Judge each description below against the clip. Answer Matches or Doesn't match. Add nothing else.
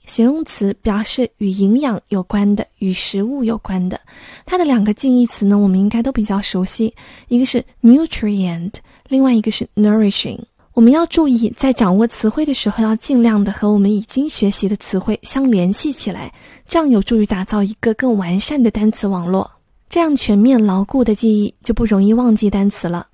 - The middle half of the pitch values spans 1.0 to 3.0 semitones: Doesn't match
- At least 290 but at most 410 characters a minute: Matches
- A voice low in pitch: Doesn't match